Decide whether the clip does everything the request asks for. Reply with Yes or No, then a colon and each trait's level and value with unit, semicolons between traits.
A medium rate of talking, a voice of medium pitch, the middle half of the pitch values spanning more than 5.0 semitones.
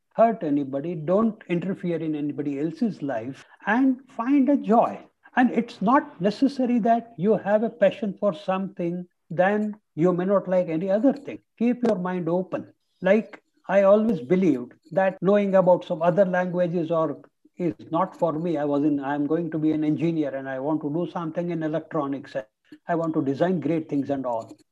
Yes: average, 185 wpm; medium, 180 Hz; wide, 5.4 semitones